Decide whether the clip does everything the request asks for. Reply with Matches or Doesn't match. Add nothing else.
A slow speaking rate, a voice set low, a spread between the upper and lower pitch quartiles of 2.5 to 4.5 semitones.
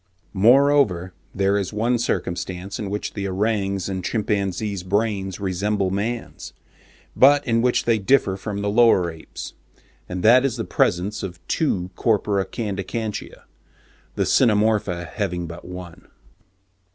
Matches